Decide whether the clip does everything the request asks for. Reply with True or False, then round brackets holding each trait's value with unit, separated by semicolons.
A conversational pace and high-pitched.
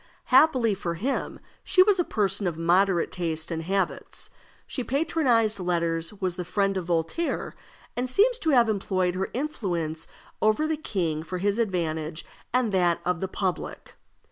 True (160 wpm; 195 Hz)